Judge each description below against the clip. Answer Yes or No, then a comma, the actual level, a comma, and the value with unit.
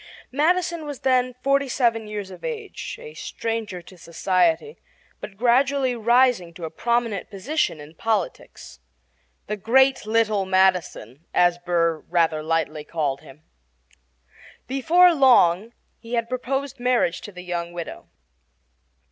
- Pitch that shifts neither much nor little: No, wide, 7.0 semitones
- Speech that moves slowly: Yes, slow, 130 wpm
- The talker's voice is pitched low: No, high, 220 Hz